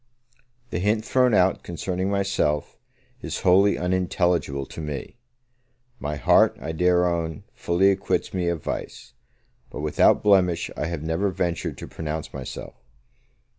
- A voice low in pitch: Yes, very low, 90 Hz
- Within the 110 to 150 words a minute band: Yes, slow, 135 wpm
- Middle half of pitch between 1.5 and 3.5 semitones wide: Yes, average, 3.0 semitones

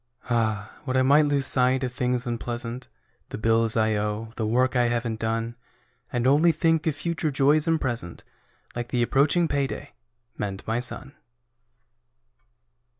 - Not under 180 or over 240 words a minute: No, average, 150 wpm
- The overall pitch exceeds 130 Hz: No, low, 125 Hz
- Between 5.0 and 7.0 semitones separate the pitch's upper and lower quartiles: No, average, 3.6 semitones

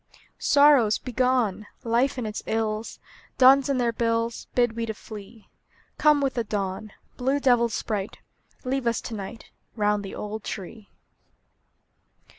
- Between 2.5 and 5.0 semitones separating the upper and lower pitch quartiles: Yes, average, 3.1 semitones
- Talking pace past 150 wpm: No, average, 140 wpm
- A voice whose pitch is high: Yes, high, 230 Hz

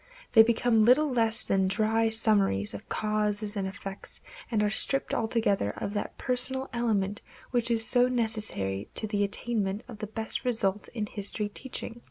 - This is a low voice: No, high, 220 Hz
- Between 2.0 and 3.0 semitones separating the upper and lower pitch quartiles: Yes, narrow, 2.6 semitones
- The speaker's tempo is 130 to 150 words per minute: No, average, 165 wpm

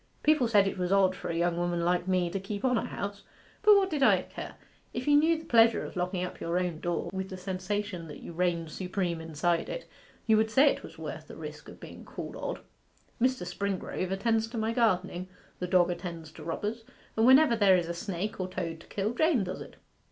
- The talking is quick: Yes, fast, 230 wpm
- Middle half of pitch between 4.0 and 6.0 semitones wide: Yes, average, 4.3 semitones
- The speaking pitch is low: No, high, 190 Hz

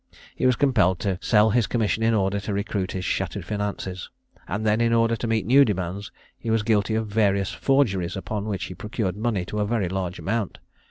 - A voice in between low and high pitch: No, low, 105 Hz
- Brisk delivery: Yes, fast, 210 wpm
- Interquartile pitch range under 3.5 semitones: Yes, average, 2.8 semitones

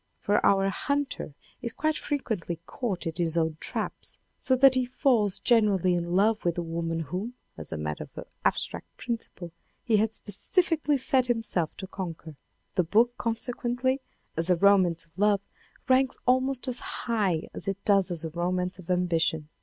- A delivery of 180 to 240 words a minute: No, average, 170 wpm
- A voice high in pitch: Yes, high, 200 Hz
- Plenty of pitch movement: Yes, wide, 6.0 semitones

